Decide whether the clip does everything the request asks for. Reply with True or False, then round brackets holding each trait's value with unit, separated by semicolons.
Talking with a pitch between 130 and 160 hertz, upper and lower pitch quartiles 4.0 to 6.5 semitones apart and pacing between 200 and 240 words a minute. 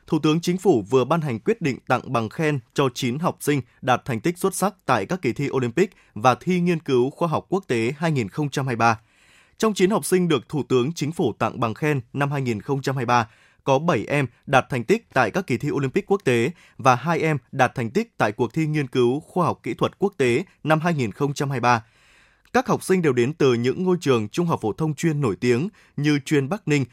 True (140 Hz; 5.1 semitones; 225 wpm)